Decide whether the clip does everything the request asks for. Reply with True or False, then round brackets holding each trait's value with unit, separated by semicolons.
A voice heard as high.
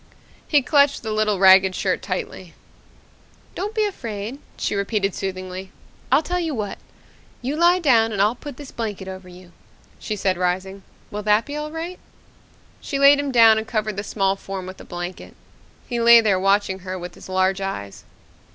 True (210 Hz)